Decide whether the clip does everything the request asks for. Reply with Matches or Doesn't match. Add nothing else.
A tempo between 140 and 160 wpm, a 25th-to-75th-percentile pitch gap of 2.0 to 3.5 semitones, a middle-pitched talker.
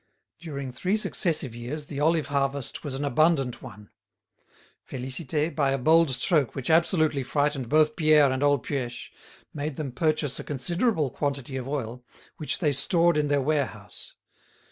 Matches